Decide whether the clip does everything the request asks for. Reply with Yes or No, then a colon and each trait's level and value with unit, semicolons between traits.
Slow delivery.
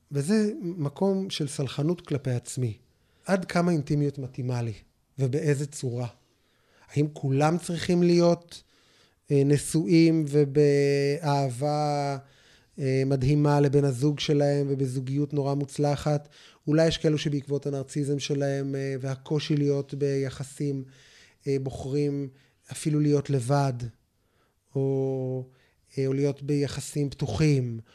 Yes: slow, 90 wpm